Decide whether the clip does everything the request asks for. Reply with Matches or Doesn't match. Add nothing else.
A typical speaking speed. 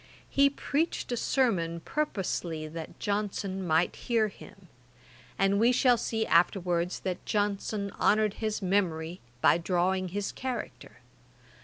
Doesn't match